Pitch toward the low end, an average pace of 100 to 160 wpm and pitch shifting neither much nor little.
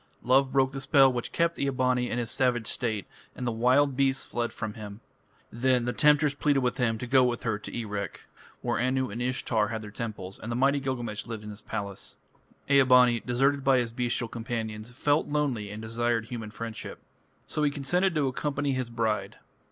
No: low, 125 Hz; average, 200 wpm; average, 3.1 semitones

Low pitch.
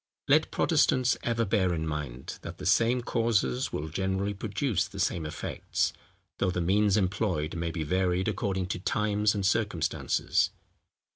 Yes: very low, 95 Hz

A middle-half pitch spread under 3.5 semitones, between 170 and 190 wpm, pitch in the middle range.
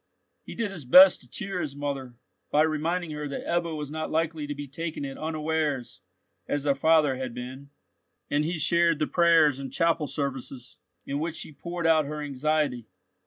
Yes: average, 2.7 semitones; average, 185 wpm; medium, 150 Hz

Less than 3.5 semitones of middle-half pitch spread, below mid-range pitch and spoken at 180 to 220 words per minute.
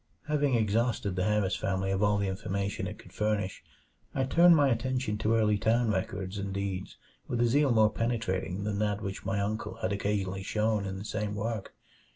Yes: narrow, 2.6 semitones; low, 105 Hz; average, 190 wpm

